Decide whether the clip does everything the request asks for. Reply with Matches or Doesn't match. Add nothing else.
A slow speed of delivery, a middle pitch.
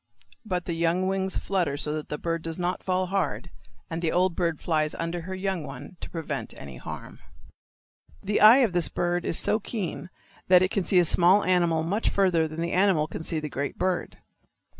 Doesn't match